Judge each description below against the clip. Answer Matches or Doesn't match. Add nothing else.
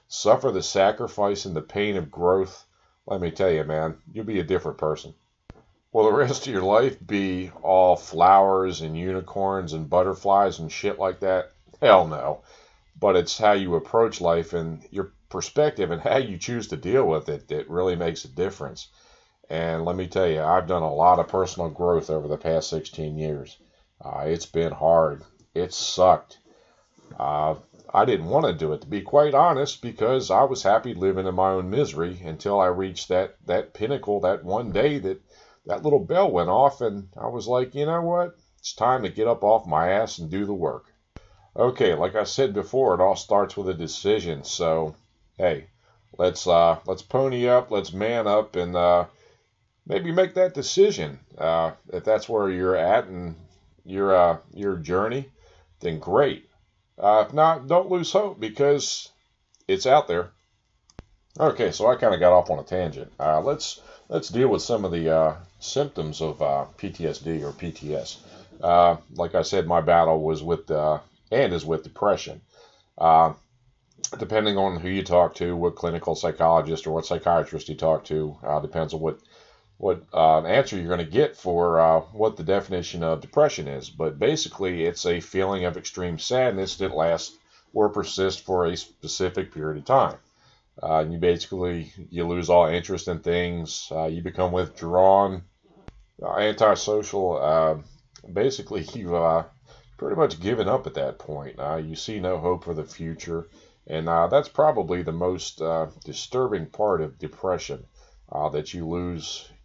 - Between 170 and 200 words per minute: Matches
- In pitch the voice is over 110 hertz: Doesn't match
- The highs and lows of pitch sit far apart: Doesn't match